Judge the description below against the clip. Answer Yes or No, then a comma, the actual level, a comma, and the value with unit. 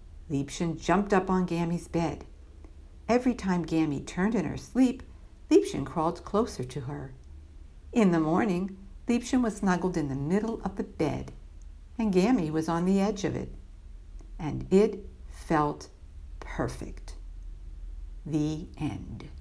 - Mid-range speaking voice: Yes, medium, 155 Hz